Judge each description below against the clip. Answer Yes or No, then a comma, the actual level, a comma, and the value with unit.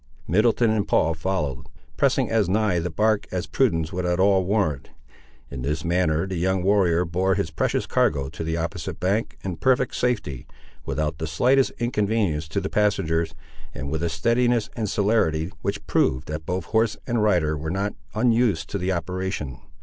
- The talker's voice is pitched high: No, very low, 90 Hz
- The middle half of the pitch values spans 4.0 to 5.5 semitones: Yes, average, 4.8 semitones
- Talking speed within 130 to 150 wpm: No, average, 175 wpm